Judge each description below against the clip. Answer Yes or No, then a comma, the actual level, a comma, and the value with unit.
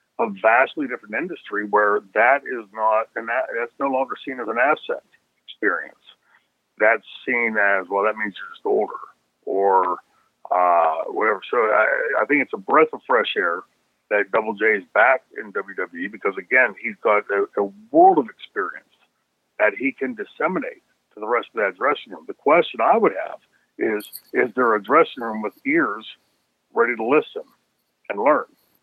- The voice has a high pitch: Yes, very high, 390 Hz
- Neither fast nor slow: Yes, average, 175 wpm